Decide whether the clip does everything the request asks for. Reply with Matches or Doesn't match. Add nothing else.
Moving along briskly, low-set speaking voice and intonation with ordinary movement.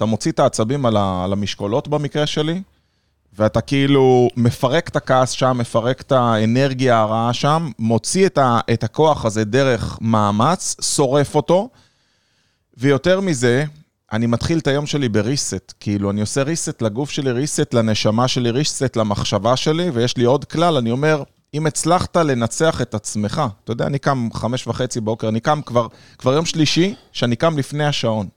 Matches